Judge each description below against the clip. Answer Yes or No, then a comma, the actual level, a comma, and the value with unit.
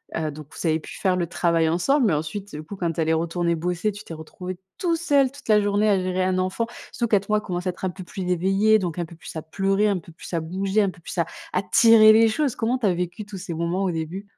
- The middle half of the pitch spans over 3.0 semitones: Yes, average, 3.8 semitones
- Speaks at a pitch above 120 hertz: Yes, medium, 185 Hz